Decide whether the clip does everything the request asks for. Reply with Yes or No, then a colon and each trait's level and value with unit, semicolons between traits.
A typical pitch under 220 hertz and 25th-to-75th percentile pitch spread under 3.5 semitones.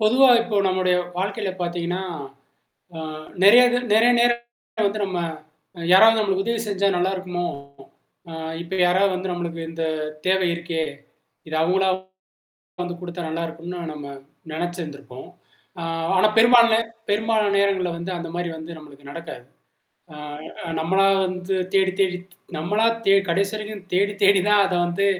Yes: medium, 185 Hz; average, 3.0 semitones